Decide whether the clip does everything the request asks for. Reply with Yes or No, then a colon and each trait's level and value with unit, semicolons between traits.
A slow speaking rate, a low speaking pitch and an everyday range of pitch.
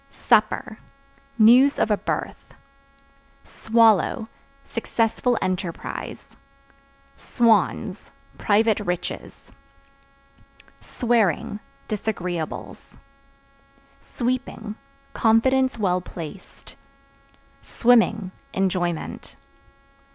No: slow, 55 wpm; high, 215 Hz; average, 3.8 semitones